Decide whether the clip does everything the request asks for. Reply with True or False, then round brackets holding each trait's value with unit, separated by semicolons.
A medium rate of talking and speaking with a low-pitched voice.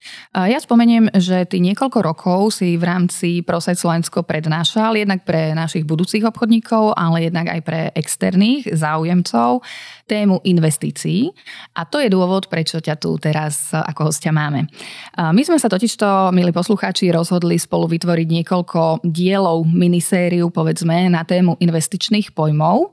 False (140 wpm; 175 Hz)